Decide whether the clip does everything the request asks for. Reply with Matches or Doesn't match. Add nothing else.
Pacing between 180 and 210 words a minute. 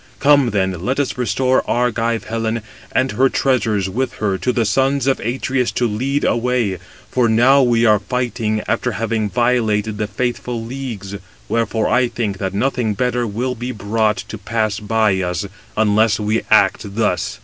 Doesn't match